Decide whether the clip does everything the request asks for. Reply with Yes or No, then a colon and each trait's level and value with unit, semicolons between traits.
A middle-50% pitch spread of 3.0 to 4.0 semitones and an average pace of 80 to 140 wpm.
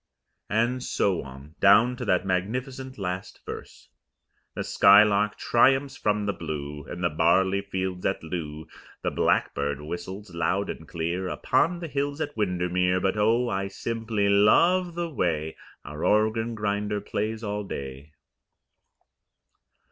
No: average, 4.4 semitones; slow, 135 wpm